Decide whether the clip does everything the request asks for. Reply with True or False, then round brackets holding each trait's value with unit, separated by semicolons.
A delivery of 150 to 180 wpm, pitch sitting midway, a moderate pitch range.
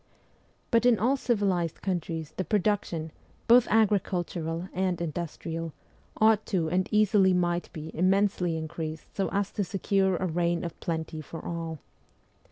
False (140 wpm; 180 Hz; 3.5 semitones)